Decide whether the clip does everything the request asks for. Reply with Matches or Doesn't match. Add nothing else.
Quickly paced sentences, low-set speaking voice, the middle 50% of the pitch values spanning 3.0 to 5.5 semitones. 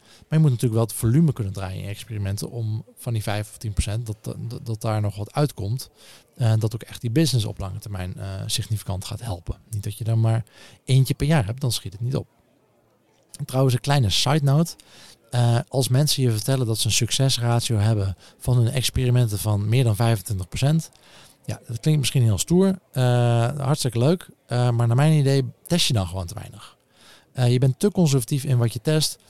Matches